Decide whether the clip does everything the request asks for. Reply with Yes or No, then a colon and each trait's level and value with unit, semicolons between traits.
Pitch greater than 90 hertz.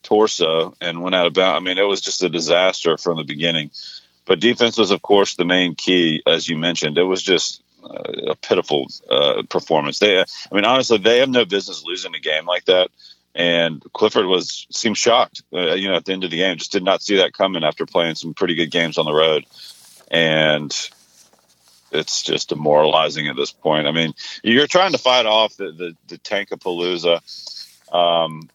No: very low, 85 Hz